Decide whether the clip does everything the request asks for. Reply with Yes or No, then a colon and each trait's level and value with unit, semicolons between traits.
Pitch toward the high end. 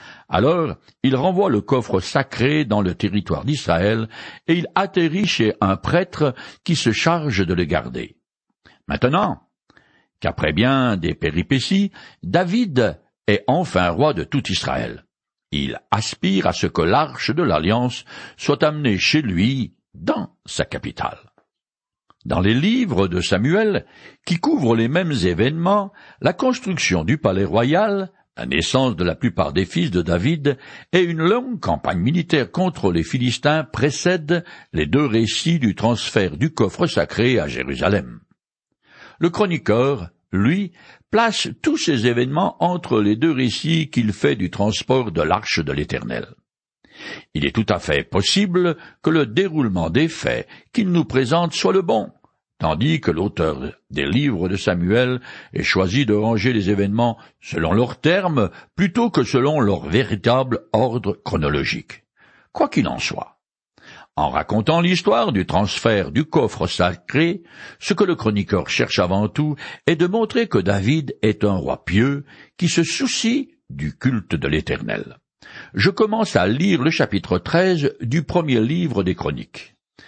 No: low, 135 Hz